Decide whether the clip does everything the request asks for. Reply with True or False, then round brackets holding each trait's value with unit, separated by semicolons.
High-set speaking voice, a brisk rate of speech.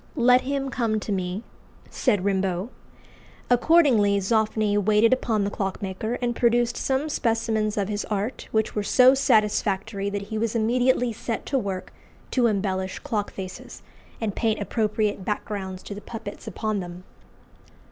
False (215 Hz; 145 wpm)